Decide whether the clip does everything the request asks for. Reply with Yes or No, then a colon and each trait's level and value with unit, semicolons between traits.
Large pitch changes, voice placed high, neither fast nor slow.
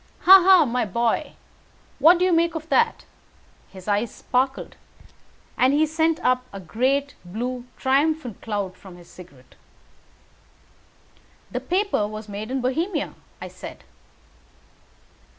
No: wide, 7.2 semitones; very high, 255 Hz; slow, 130 wpm